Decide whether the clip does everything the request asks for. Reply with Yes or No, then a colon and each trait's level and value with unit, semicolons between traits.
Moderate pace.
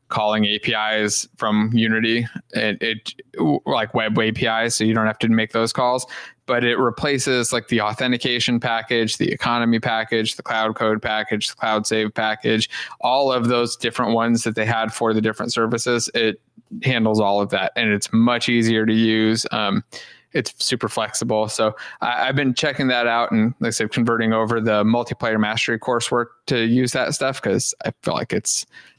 Yes: average, 185 wpm